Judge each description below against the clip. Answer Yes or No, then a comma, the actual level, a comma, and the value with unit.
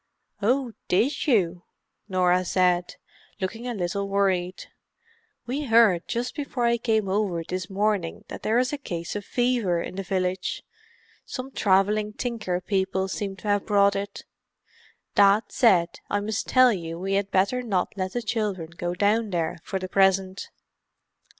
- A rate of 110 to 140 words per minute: No, average, 150 wpm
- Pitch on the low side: No, high, 200 Hz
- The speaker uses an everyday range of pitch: Yes, average, 3.4 semitones